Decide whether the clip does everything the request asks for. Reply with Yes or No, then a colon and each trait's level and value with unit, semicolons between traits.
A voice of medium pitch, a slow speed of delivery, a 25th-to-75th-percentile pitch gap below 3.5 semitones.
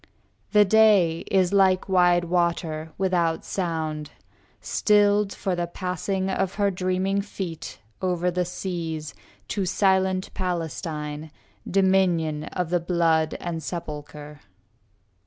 Yes: medium, 180 Hz; slow, 110 wpm; average, 2.7 semitones